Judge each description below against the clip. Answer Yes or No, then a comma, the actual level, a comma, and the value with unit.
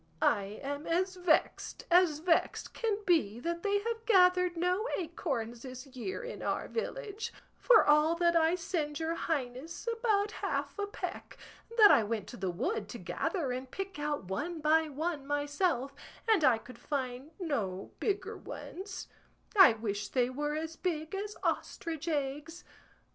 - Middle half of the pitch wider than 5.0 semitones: Yes, wide, 5.5 semitones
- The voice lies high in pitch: Yes, very high, 320 Hz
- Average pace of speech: Yes, average, 160 wpm